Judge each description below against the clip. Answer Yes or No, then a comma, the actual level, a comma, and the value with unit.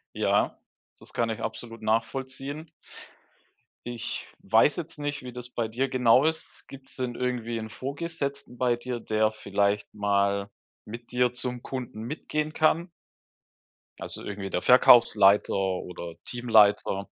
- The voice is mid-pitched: No, low, 120 Hz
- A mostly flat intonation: No, average, 3.6 semitones